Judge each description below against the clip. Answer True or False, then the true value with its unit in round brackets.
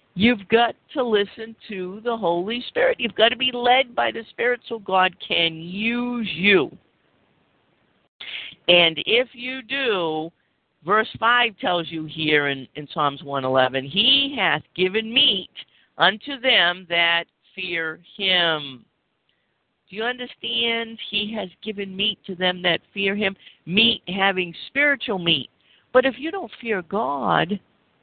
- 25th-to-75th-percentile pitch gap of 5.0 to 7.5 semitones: True (5.6 semitones)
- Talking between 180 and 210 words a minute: False (140 wpm)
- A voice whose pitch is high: True (200 Hz)